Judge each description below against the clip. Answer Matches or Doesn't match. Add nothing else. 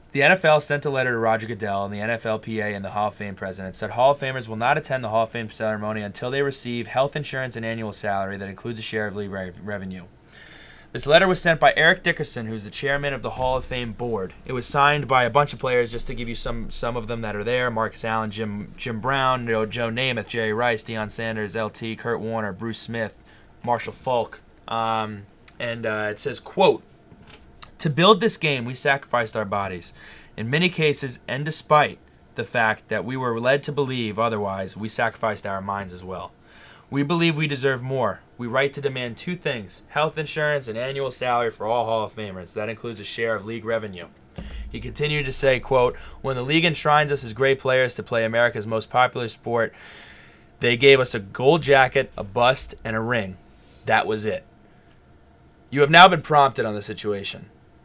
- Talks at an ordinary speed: Doesn't match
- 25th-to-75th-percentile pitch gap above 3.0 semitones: Matches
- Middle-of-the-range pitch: Doesn't match